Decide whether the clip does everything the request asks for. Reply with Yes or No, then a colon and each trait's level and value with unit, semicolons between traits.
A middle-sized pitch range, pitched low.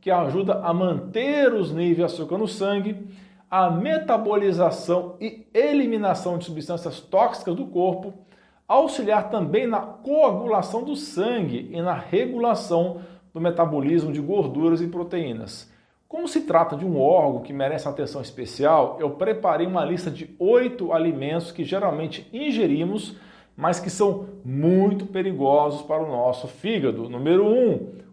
No: average, 4.3 semitones; medium, 180 Hz